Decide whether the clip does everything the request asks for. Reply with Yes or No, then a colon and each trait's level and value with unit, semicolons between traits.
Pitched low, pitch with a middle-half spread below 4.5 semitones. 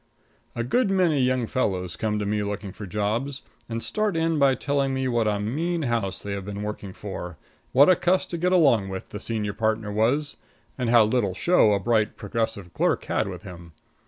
No: low, 110 Hz; wide, 5.4 semitones